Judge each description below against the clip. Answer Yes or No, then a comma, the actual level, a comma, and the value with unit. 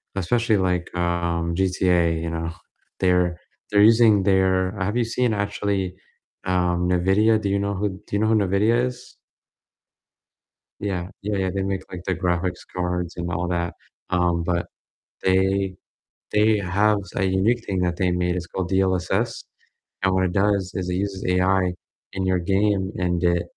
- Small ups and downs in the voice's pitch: Yes, narrow, 2.2 semitones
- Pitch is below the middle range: Yes, very low, 95 Hz